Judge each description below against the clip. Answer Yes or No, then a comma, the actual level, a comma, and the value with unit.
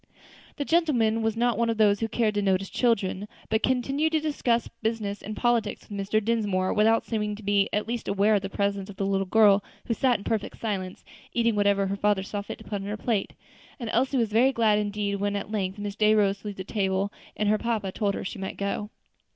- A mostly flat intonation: Yes, narrow, 2.3 semitones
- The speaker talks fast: Yes, fast, 240 wpm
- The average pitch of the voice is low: No, high, 210 Hz